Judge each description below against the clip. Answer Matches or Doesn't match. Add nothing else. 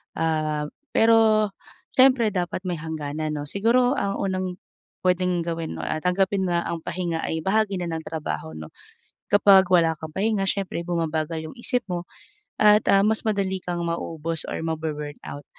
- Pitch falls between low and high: Matches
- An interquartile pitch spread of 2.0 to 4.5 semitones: Matches